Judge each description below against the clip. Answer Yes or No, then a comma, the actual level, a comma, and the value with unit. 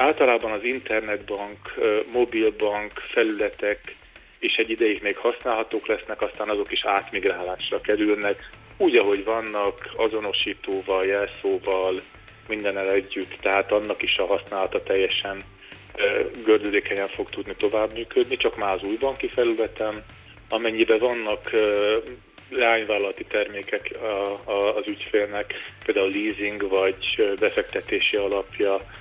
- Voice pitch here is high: No, low, 115 Hz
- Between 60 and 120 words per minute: Yes, slow, 105 wpm